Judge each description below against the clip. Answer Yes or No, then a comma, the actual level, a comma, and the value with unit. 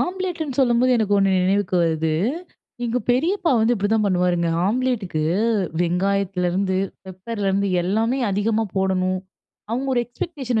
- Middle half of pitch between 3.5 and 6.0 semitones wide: Yes, average, 4.7 semitones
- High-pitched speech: Yes, high, 205 Hz